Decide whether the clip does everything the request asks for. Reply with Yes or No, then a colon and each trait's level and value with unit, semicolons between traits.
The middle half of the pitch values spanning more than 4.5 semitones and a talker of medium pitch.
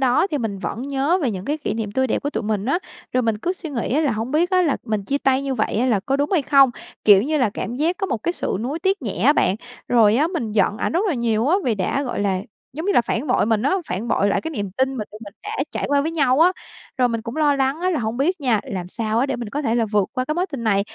No: wide, 5.5 semitones; very high, 255 Hz